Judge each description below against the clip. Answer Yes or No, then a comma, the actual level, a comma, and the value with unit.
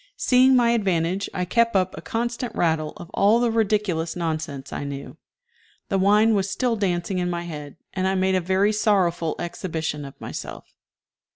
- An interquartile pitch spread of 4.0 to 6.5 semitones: Yes, average, 4.3 semitones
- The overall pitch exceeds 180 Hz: Yes, high, 190 Hz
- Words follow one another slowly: No, average, 175 wpm